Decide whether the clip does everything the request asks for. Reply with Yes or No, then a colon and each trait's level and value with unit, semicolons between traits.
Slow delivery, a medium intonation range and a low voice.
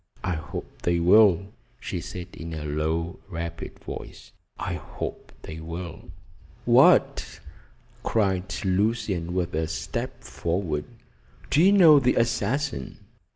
Yes: slow, 120 wpm; average, 4.3 semitones; very low, 90 Hz